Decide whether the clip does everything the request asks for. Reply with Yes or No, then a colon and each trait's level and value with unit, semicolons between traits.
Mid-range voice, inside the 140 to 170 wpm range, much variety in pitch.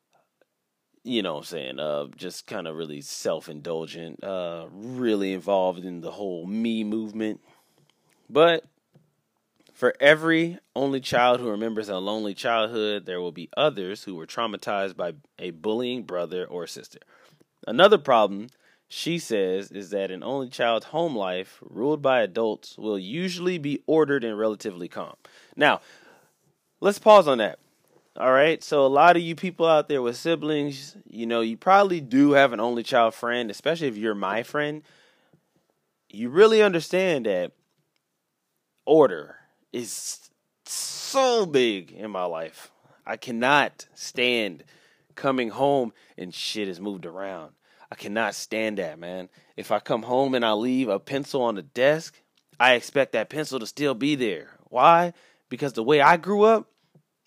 No: low, 125 Hz; average, 155 wpm; wide, 7.1 semitones